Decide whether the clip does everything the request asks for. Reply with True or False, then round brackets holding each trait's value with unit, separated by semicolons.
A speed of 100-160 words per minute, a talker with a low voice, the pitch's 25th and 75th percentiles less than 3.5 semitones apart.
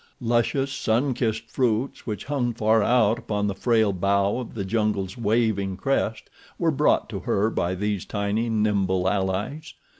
True (155 wpm; 110 Hz; 2.9 semitones)